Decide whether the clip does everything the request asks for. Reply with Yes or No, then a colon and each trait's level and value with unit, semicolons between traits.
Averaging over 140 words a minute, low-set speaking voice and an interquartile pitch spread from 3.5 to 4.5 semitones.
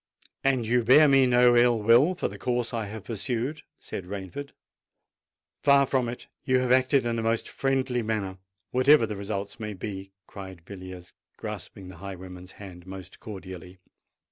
No: average, 160 wpm; low, 110 Hz; average, 4.9 semitones